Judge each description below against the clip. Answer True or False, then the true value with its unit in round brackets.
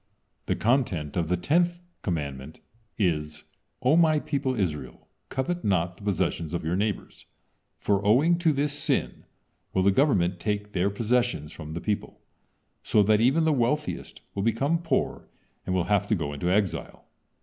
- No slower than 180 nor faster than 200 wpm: False (160 wpm)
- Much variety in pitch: True (7.5 semitones)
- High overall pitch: False (105 Hz)